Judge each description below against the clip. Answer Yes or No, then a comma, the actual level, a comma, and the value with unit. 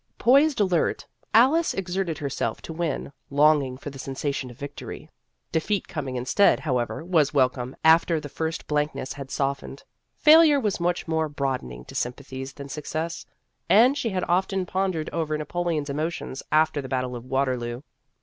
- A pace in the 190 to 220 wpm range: No, average, 160 wpm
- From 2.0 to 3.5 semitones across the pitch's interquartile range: No, average, 4.7 semitones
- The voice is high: No, medium, 150 Hz